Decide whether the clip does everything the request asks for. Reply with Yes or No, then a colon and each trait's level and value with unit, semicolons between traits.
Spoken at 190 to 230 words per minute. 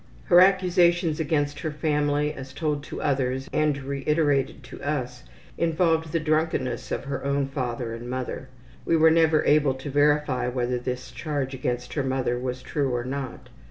No: average, 165 wpm